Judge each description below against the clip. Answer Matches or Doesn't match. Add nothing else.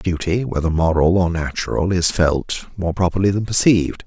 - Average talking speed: Matches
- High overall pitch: Doesn't match